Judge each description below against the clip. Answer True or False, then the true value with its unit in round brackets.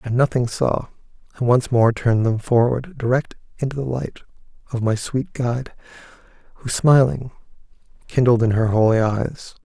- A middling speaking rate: True (150 wpm)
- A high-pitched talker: False (120 Hz)